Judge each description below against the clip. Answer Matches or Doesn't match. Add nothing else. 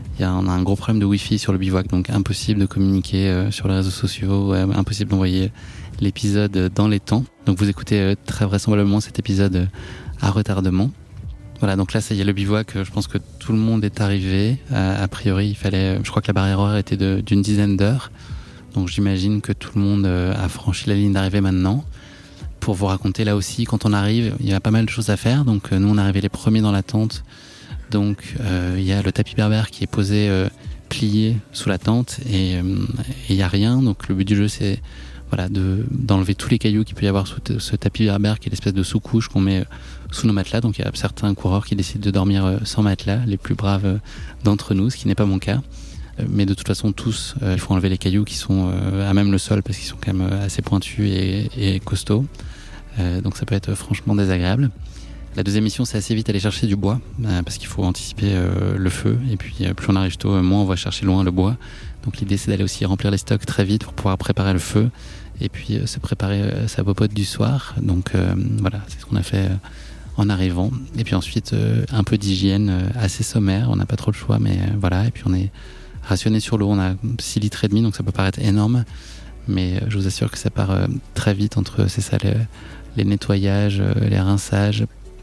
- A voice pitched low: Matches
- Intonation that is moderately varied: Doesn't match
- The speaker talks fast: Matches